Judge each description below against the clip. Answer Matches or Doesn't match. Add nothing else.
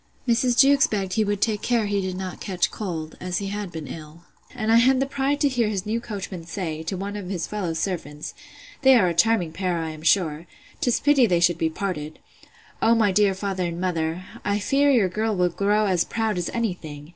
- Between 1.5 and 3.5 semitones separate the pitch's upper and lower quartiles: Doesn't match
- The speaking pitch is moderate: Doesn't match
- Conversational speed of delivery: Doesn't match